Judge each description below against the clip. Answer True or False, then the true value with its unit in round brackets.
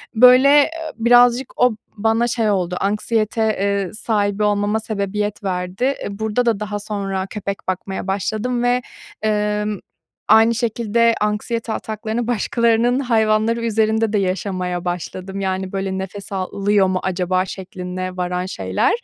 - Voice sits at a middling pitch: False (210 Hz)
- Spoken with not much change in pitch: False (3.0 semitones)